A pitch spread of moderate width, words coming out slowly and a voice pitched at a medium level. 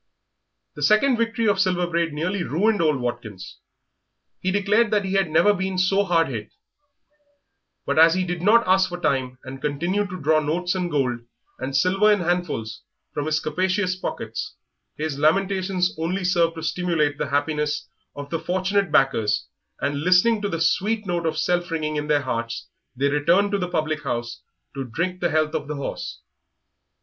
No: average, 4.2 semitones; average, 180 wpm; medium, 170 Hz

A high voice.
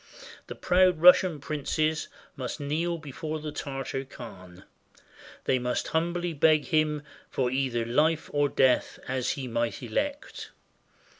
No: medium, 145 Hz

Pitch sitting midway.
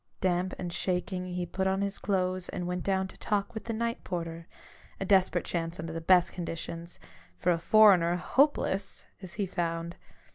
Yes: medium, 180 Hz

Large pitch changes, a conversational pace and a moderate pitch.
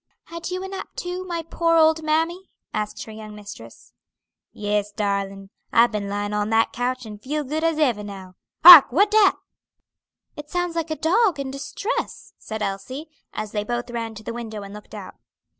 No: wide, 7.8 semitones; average, 190 wpm; high, 240 Hz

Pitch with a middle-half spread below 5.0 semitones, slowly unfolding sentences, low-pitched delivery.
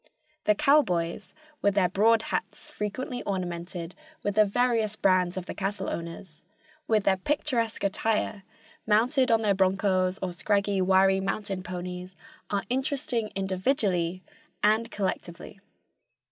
No: average, 2.9 semitones; slow, 125 wpm; high, 195 Hz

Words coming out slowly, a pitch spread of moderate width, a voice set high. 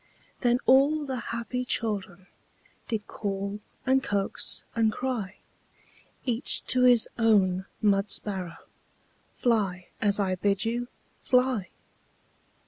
Yes: slow, 110 wpm; average, 4.0 semitones; high, 220 Hz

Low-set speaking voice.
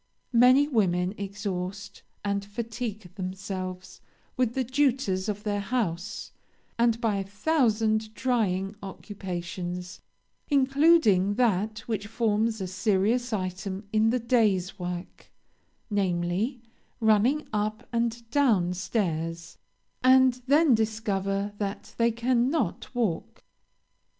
No: high, 210 Hz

